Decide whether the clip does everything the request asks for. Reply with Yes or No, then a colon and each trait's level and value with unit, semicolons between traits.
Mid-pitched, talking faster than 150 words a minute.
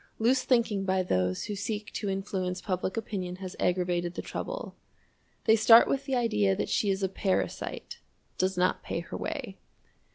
No: high, 195 Hz; average, 170 wpm